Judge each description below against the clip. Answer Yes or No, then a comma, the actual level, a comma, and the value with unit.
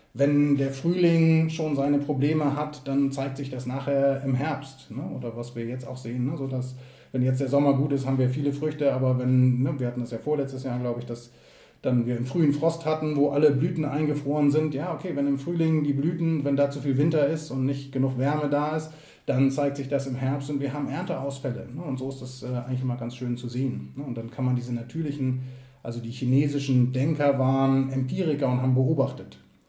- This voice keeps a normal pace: No, fast, 230 wpm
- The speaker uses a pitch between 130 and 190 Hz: Yes, low, 135 Hz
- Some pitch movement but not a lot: No, narrow, 2.2 semitones